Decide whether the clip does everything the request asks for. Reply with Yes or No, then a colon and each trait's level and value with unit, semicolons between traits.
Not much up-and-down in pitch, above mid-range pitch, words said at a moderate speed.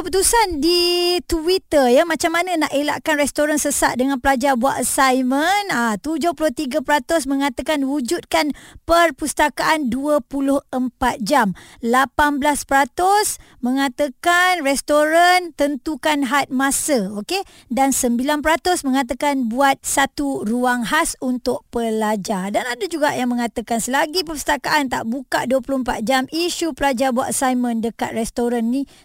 No: average, 3.5 semitones; very high, 285 Hz; average, 115 wpm